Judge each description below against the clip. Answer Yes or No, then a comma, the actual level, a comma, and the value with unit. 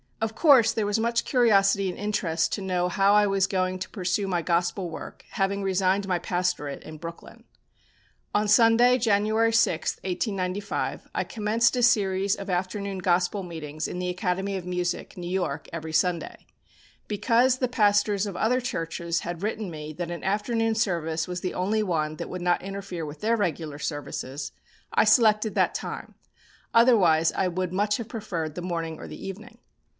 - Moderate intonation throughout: Yes, average, 3.5 semitones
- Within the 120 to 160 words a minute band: No, average, 175 wpm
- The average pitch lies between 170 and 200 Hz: Yes, high, 190 Hz